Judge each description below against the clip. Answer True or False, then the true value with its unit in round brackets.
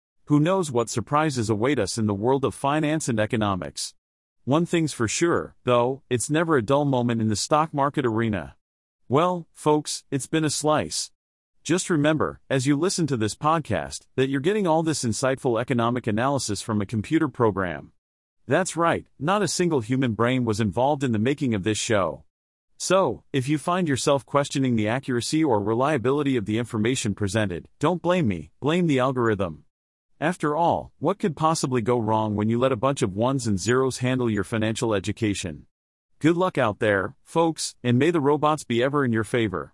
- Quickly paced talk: False (185 wpm)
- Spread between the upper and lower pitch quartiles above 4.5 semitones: True (5.6 semitones)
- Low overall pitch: True (130 Hz)